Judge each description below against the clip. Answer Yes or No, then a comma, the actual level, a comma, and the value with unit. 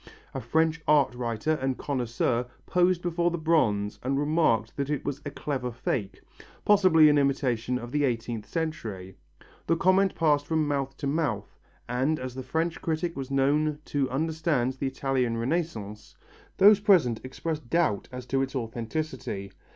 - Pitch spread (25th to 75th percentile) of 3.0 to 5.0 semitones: Yes, average, 4.7 semitones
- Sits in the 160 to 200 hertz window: No, medium, 140 Hz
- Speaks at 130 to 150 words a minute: No, average, 160 wpm